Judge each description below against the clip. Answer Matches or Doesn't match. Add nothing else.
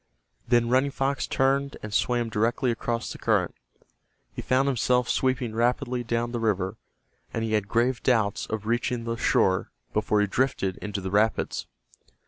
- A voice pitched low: Matches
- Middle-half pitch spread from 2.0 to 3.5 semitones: Matches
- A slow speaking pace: Doesn't match